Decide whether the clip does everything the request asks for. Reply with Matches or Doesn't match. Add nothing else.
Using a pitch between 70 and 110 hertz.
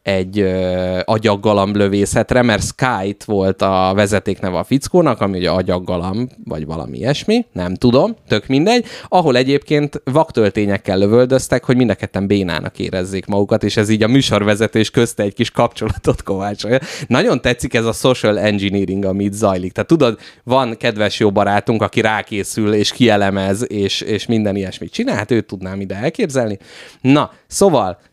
Matches